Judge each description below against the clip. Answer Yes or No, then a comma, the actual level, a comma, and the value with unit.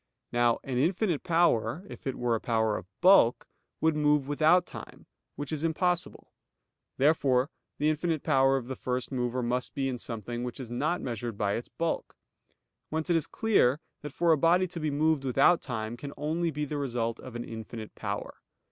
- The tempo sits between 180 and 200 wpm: Yes, average, 190 wpm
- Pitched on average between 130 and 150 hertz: Yes, low, 135 Hz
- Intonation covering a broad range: No, average, 4.8 semitones